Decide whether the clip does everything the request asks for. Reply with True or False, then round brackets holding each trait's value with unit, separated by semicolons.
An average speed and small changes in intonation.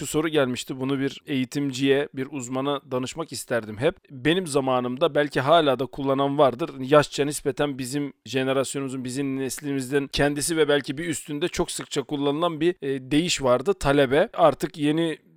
False (150 wpm; 2.2 semitones)